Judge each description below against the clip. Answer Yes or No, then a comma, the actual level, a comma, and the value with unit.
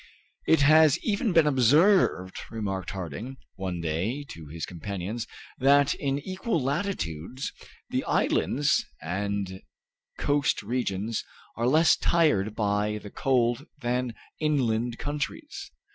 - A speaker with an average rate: No, slow, 115 wpm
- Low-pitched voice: Yes, low, 120 Hz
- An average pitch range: No, wide, 6.6 semitones